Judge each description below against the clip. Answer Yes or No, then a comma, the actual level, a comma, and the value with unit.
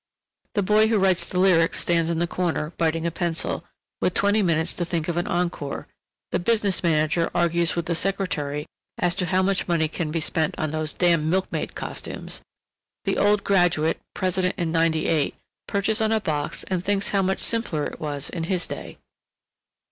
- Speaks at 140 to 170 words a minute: No, average, 185 wpm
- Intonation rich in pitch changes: No, average, 2.9 semitones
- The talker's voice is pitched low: No, medium, 175 Hz